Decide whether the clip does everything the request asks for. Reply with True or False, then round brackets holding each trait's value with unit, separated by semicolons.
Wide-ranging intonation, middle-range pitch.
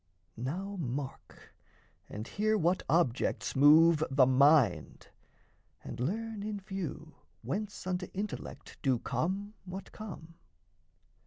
True (6.1 semitones; 170 Hz)